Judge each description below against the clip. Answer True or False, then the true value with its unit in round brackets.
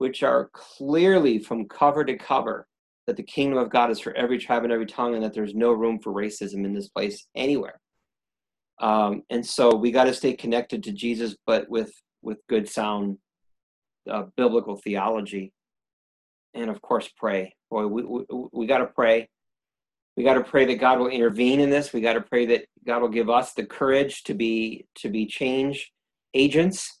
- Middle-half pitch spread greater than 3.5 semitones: False (3.2 semitones)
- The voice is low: True (120 Hz)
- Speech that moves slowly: False (190 wpm)